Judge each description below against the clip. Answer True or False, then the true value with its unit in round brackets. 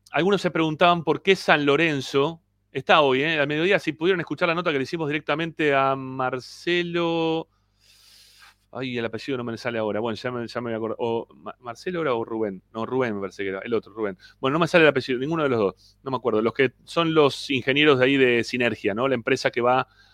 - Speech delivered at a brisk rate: True (225 wpm)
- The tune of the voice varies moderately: False (5.8 semitones)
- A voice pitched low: True (130 Hz)